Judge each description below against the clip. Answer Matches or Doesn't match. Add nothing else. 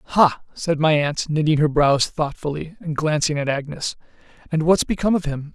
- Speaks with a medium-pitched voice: Matches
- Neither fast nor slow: Matches